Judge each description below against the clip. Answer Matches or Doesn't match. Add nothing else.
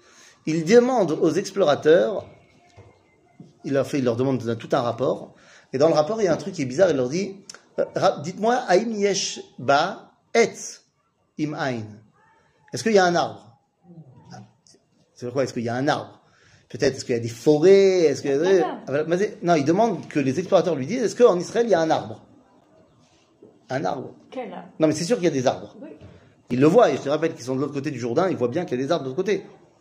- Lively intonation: Matches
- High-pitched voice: Doesn't match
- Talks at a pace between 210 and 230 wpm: Matches